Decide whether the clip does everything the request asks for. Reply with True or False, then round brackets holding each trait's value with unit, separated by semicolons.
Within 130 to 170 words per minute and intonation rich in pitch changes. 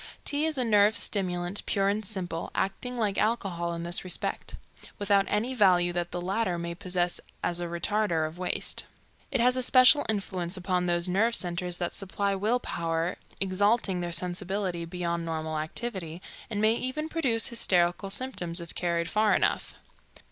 False (165 wpm; 3.7 semitones)